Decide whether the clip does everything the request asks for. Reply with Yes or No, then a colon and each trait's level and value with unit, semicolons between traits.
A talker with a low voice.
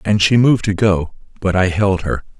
Yes: very low, 95 Hz